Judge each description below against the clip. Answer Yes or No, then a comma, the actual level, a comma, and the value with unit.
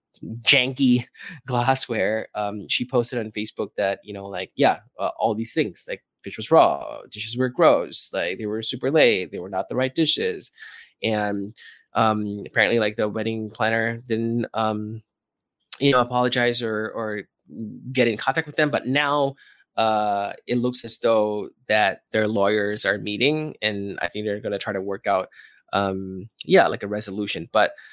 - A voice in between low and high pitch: No, low, 110 Hz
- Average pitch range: Yes, average, 3.1 semitones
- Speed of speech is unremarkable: Yes, average, 175 wpm